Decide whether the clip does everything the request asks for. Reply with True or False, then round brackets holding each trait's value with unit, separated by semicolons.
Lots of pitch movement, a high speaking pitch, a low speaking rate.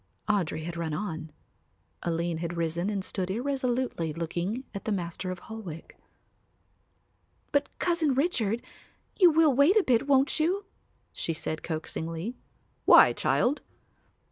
True (8.1 semitones; 200 Hz; 130 wpm)